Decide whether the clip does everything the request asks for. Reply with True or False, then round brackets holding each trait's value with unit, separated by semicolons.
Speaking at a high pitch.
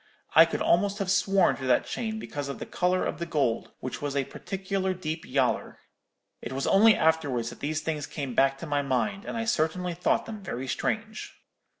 False (160 Hz)